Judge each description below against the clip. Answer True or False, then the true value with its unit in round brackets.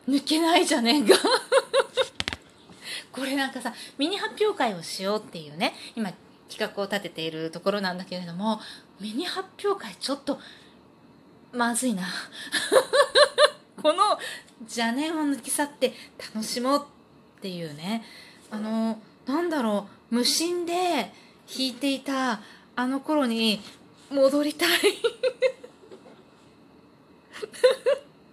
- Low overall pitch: False (265 Hz)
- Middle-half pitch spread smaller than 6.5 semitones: False (7.2 semitones)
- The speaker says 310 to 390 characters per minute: False (215 characters per minute)